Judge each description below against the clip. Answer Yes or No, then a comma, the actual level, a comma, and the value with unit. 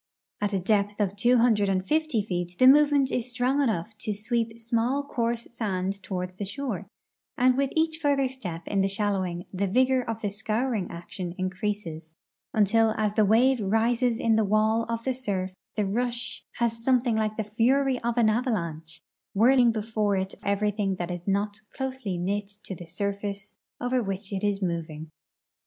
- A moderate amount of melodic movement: Yes, average, 3.8 semitones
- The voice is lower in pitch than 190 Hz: No, high, 215 Hz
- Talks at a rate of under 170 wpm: No, average, 175 wpm